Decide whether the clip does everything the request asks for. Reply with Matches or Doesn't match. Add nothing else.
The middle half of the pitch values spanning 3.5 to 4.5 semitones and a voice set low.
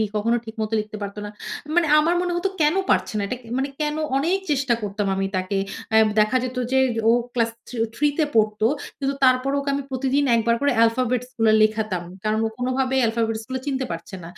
Doesn't match